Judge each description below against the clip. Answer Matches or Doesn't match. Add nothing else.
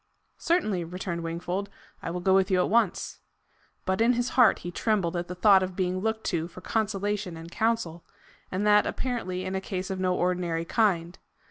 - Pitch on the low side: Doesn't match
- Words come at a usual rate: Matches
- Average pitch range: Matches